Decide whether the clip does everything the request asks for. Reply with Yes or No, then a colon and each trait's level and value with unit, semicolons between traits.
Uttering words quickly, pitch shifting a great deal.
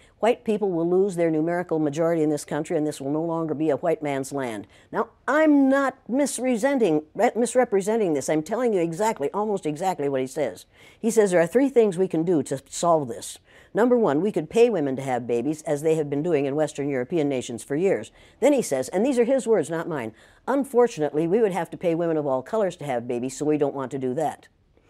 Yes: fast, 230 wpm; wide, 7.3 semitones